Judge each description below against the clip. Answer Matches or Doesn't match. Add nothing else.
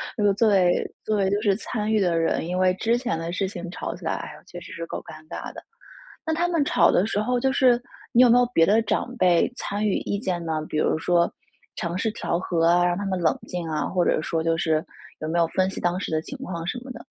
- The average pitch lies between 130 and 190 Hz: Matches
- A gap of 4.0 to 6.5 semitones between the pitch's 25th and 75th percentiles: Matches